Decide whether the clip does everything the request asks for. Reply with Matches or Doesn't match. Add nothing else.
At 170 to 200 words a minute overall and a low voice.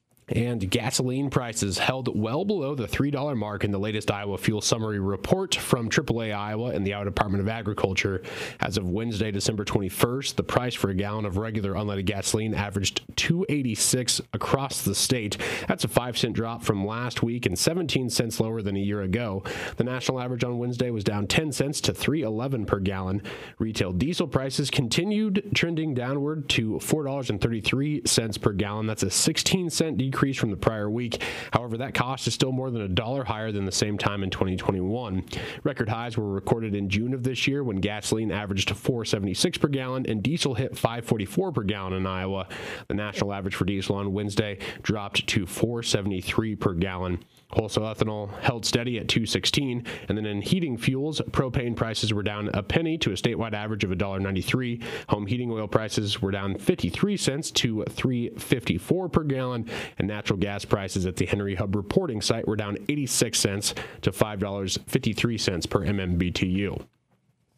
Matches